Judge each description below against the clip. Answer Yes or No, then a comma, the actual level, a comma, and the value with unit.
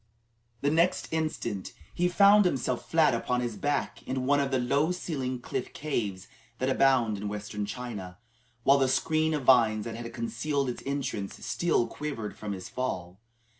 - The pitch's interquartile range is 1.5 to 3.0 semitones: No, average, 4.7 semitones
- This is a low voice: Yes, low, 130 Hz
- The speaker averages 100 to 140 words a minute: No, average, 170 wpm